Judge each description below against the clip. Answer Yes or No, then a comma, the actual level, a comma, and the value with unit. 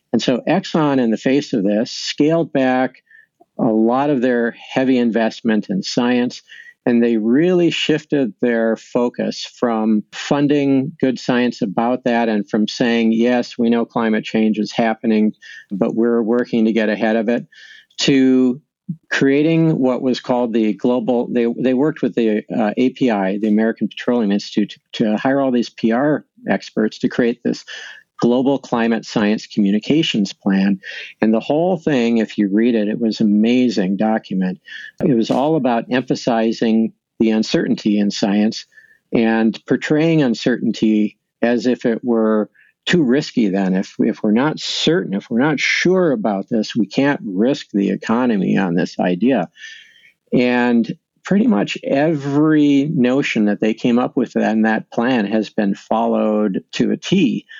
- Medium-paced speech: Yes, average, 155 wpm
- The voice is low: Yes, low, 120 Hz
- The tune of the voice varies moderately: Yes, average, 3.8 semitones